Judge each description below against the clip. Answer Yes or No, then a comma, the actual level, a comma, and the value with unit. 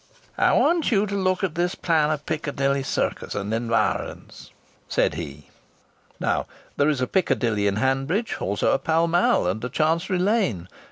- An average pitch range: No, wide, 7.7 semitones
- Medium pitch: Yes, medium, 150 Hz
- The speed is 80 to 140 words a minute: No, average, 165 wpm